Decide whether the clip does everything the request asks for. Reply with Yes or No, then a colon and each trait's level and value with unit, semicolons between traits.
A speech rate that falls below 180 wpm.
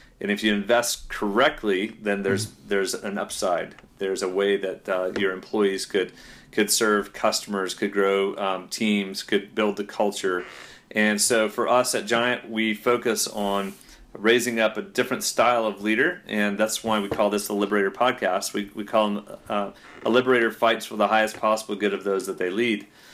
No: average, 185 wpm